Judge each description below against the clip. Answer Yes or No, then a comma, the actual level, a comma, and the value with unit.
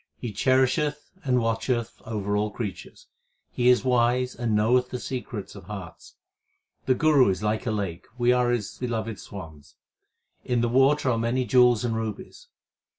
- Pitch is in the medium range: No, low, 120 Hz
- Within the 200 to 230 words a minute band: No, average, 160 wpm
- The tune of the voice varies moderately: Yes, average, 3.0 semitones